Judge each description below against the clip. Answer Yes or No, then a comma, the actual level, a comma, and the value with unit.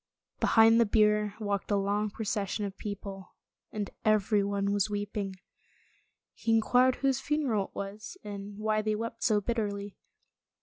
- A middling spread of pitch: No, narrow, 1.6 semitones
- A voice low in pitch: No, high, 210 Hz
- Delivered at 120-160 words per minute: Yes, average, 140 wpm